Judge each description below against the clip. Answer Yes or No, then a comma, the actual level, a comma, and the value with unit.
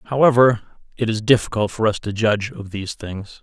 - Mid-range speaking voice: No, low, 110 Hz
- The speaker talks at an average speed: Yes, average, 195 wpm